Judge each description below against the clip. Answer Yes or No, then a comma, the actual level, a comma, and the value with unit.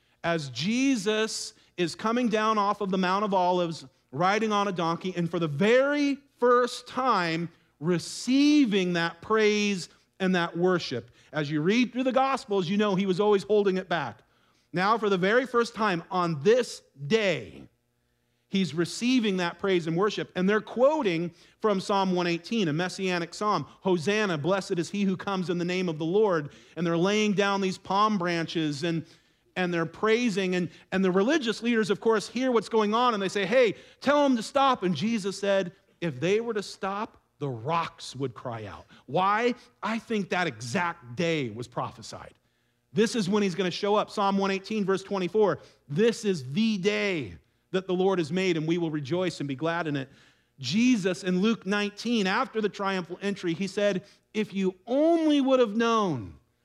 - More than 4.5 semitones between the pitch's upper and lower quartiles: No, average, 4.2 semitones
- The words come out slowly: No, average, 185 wpm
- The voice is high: Yes, high, 195 Hz